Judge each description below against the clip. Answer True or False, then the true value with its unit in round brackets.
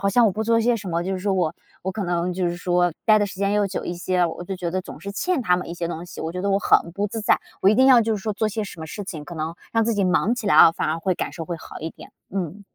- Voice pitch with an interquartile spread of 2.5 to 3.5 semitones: True (3.2 semitones)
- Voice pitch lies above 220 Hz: False (190 Hz)